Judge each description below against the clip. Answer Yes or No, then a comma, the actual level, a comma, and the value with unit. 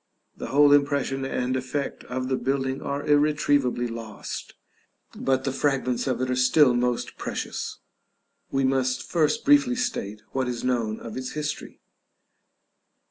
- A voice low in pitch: Yes, low, 130 Hz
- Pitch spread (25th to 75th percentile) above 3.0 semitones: No, narrow, 2.4 semitones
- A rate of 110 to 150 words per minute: Yes, average, 140 wpm